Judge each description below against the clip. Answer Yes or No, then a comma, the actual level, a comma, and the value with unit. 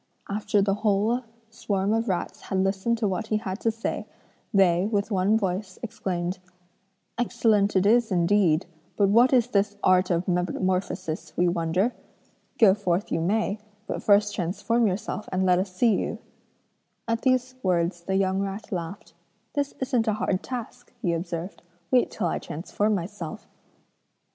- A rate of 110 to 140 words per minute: No, average, 160 wpm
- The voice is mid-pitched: No, high, 200 Hz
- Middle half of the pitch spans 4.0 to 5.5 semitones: No, average, 3.1 semitones